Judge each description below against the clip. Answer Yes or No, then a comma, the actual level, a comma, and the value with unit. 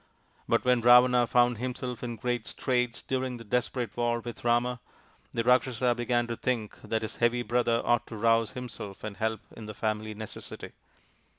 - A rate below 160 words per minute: No, average, 175 wpm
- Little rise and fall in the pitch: Yes, narrow, 1.6 semitones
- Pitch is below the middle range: Yes, low, 120 Hz